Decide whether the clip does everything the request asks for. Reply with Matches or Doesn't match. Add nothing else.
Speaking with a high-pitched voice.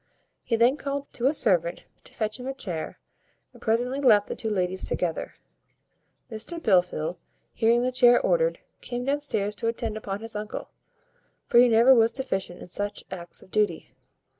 Matches